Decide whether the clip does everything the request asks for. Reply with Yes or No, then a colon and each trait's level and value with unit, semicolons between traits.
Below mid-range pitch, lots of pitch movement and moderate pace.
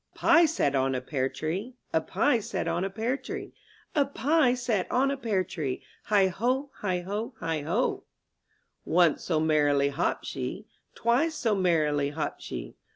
No: high, 190 Hz; wide, 8.3 semitones; average, 180 wpm